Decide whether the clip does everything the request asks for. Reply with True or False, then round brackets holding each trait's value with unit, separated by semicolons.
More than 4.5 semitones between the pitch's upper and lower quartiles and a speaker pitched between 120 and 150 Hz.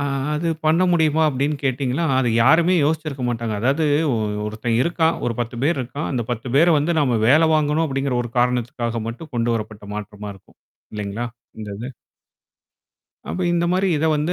True (5.2 semitones; 135 Hz)